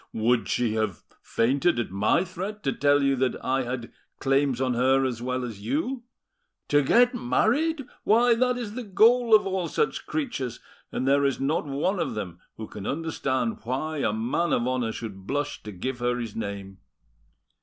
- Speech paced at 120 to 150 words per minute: No, average, 185 wpm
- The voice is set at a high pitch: No, low, 135 Hz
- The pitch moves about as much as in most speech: No, wide, 8.2 semitones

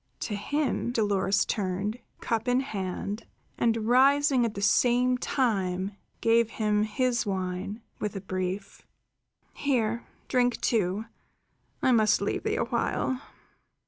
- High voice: Yes, high, 220 Hz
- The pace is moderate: No, slow, 125 wpm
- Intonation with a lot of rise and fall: No, average, 3.8 semitones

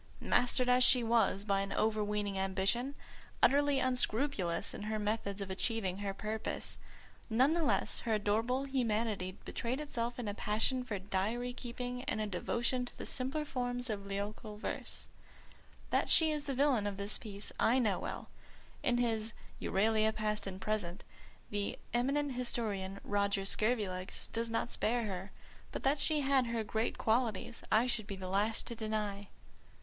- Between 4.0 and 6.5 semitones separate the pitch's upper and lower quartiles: No, average, 3.5 semitones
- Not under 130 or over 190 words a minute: Yes, average, 160 wpm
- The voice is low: No, high, 220 Hz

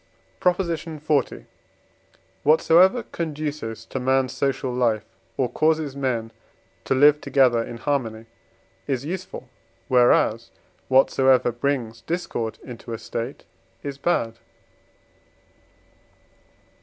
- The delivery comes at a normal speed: No, slow, 95 wpm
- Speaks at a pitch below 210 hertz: Yes, low, 135 Hz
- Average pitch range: Yes, average, 4.5 semitones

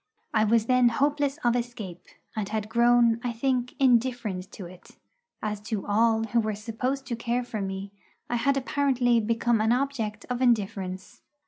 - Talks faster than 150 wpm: Yes, average, 165 wpm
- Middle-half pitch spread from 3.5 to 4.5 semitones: No, average, 2.7 semitones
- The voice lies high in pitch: Yes, high, 230 Hz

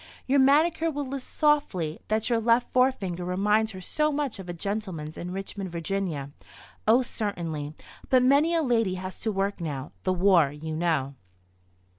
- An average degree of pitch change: No, wide, 6.8 semitones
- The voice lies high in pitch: Yes, high, 200 Hz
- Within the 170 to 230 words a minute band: No, average, 160 wpm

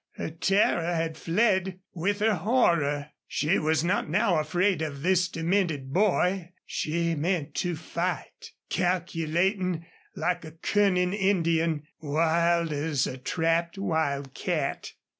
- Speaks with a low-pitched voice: No, medium, 170 Hz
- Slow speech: Yes, slow, 120 wpm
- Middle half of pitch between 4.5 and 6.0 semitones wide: No, average, 2.7 semitones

